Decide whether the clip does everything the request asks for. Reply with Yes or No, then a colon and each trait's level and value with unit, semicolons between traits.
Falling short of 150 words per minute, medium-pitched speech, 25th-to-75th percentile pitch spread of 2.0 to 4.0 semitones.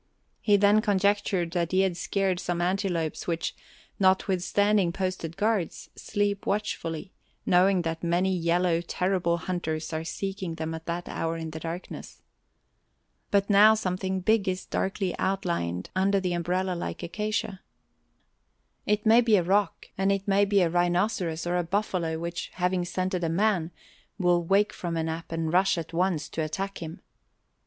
No: average, 160 wpm; medium, 180 Hz; average, 2.7 semitones